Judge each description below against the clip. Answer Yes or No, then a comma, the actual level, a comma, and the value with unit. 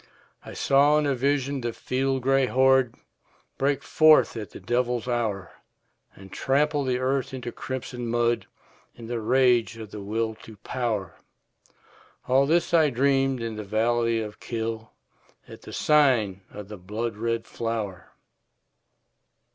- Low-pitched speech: Yes, low, 120 Hz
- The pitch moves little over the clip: No, average, 3.2 semitones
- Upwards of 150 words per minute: No, average, 145 wpm